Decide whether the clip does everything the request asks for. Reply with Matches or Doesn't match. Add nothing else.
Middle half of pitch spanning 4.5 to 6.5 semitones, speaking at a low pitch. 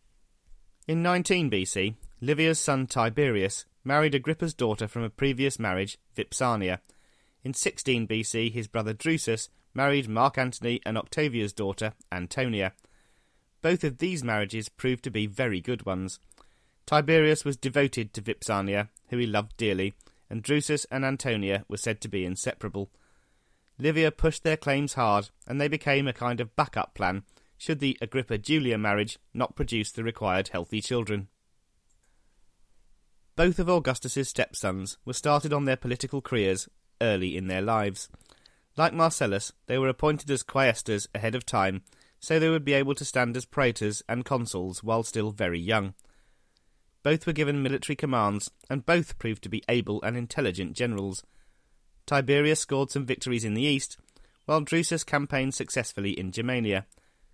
Matches